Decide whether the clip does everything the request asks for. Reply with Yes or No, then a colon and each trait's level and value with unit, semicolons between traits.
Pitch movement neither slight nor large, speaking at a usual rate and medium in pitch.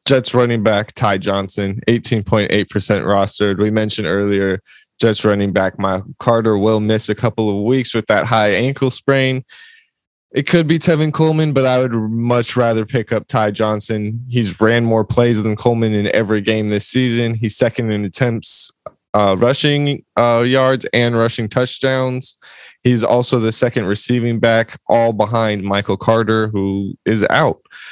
No: average, 3.0 semitones; average, 170 wpm; low, 115 Hz